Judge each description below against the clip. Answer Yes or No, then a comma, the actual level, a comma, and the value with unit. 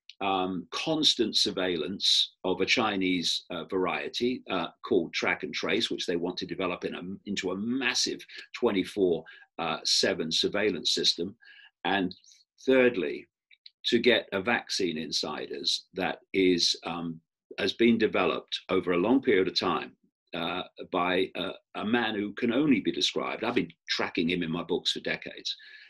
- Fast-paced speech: No, average, 155 wpm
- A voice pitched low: Yes, low, 115 Hz